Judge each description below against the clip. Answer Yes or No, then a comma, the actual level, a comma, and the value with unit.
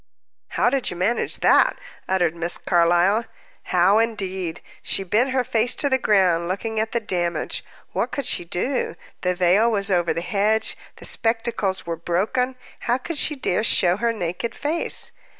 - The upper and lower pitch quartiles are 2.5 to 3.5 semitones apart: No, average, 5.0 semitones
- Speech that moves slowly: No, average, 170 wpm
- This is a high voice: Yes, high, 200 Hz